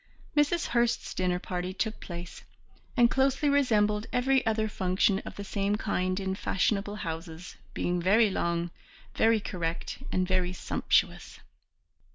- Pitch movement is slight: No, average, 3.7 semitones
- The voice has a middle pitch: No, high, 200 Hz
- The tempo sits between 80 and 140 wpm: Yes, slow, 135 wpm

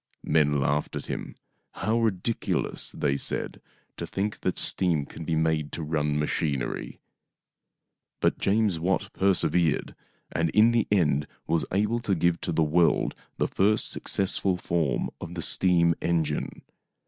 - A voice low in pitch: Yes, very low, 85 Hz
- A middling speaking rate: Yes, average, 155 wpm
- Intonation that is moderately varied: Yes, average, 4.2 semitones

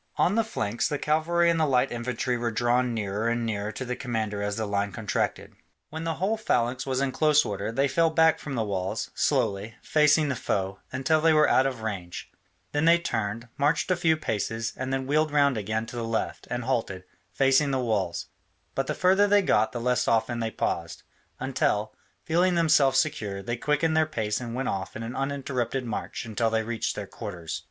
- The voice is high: No, low, 125 Hz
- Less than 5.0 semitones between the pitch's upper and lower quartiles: No, average, 5.3 semitones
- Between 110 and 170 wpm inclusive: No, fast, 205 wpm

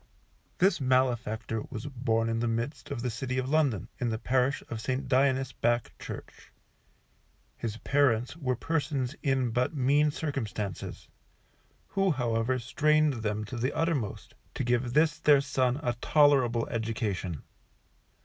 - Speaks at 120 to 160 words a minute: Yes, average, 140 wpm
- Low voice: Yes, low, 125 Hz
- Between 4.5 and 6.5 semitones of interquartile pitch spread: No, average, 3.6 semitones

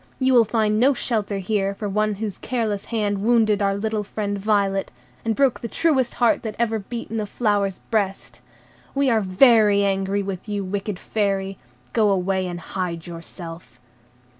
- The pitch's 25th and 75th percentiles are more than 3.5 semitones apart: No, narrow, 2.4 semitones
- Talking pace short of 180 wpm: Yes, average, 170 wpm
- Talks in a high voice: Yes, high, 205 Hz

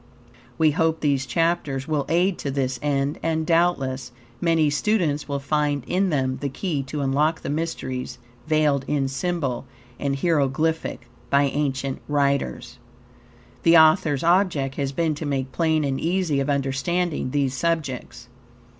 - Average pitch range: Yes, average, 3.2 semitones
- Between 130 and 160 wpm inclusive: Yes, average, 145 wpm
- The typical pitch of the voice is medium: Yes, medium, 145 Hz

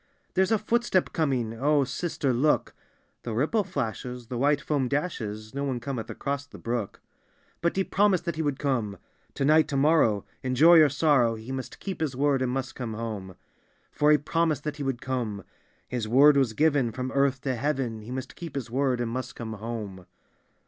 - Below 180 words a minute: No, fast, 205 wpm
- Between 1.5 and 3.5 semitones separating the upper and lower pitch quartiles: No, average, 4.1 semitones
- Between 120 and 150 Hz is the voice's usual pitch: Yes, low, 135 Hz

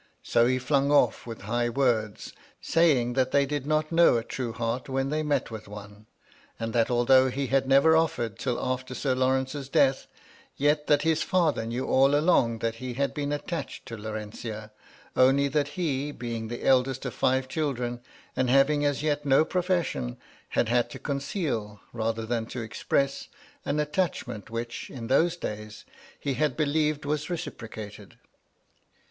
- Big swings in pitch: No, average, 3.9 semitones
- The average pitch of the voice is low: Yes, low, 130 Hz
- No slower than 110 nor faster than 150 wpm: No, average, 165 wpm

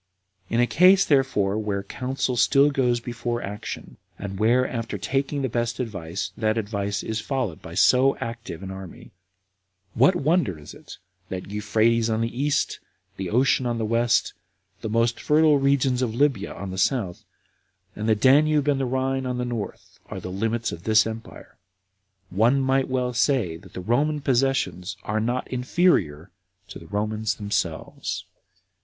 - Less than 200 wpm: Yes, average, 165 wpm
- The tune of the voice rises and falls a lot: No, average, 4.2 semitones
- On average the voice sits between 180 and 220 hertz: No, low, 115 Hz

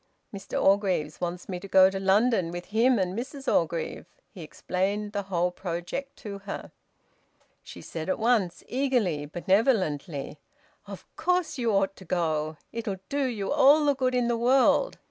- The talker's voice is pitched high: Yes, high, 200 Hz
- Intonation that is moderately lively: No, wide, 5.7 semitones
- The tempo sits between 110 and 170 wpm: Yes, average, 165 wpm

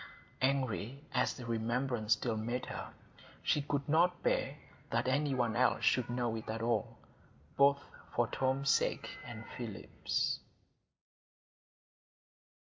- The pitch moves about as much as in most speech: Yes, average, 3.0 semitones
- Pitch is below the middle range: Yes, low, 125 Hz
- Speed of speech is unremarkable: No, slow, 120 wpm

